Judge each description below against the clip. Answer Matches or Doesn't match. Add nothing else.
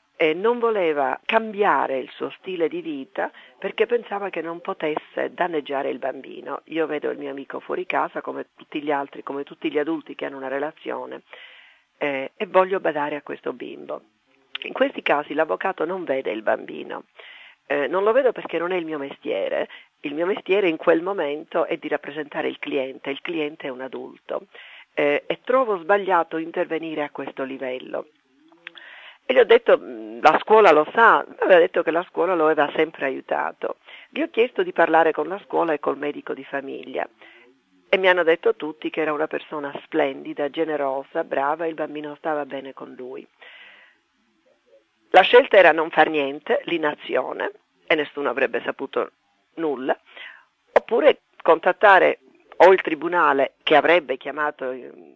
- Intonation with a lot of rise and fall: Matches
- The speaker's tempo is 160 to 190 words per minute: Matches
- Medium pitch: Matches